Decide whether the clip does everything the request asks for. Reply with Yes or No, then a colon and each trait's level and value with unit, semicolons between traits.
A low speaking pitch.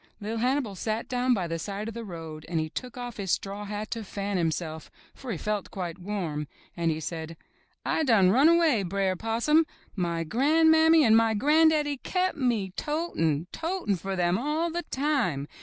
No: high, 215 Hz